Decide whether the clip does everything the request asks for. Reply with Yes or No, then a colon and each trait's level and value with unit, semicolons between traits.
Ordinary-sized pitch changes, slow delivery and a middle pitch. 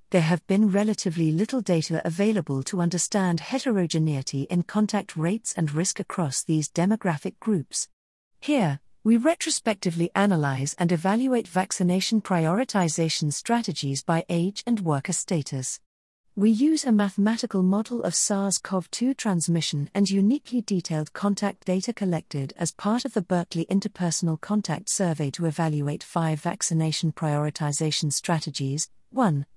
Yes: average, 4.2 semitones; slow, 130 wpm; medium, 180 Hz